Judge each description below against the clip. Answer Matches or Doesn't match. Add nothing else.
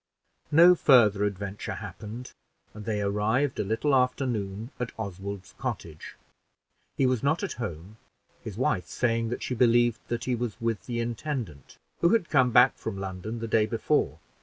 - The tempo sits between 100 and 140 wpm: Doesn't match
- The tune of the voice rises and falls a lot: Doesn't match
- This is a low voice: Matches